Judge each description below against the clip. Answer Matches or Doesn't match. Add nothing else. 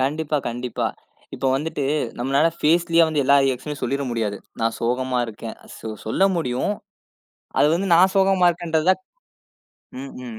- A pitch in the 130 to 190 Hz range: Matches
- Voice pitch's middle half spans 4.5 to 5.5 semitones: Matches